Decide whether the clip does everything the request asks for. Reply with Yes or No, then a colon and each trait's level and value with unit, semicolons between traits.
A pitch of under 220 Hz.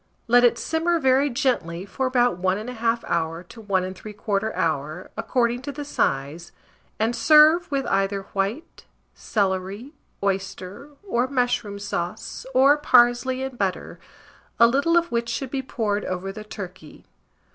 No: high, 230 Hz